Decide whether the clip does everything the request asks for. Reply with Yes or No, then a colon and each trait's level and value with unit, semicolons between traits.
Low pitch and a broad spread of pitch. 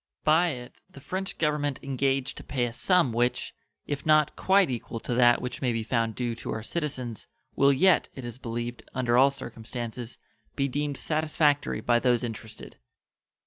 No: low, 130 Hz; average, 3.6 semitones